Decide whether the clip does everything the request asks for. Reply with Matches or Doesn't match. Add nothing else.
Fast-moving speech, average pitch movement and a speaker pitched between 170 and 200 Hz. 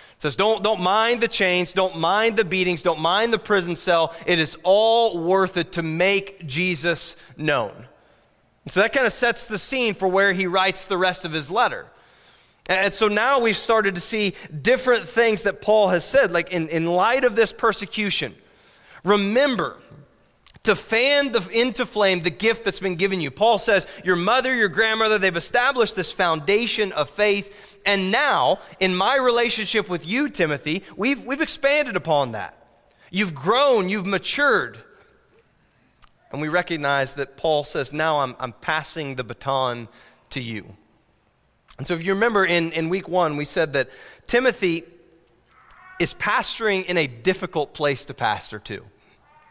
Doesn't match